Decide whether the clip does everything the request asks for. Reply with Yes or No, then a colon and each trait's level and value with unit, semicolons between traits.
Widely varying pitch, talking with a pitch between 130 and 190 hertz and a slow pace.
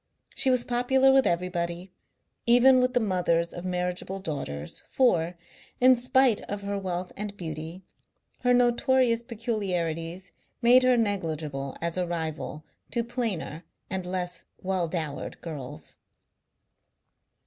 Yes: wide, 6.1 semitones; medium, 185 Hz; slow, 125 wpm